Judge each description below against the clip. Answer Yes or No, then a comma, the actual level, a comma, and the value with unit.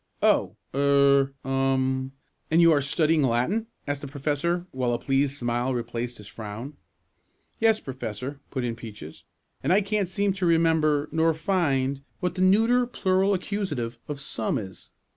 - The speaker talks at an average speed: Yes, average, 155 wpm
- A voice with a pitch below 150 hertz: Yes, medium, 140 Hz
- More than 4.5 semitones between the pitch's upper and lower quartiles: Yes, average, 5.1 semitones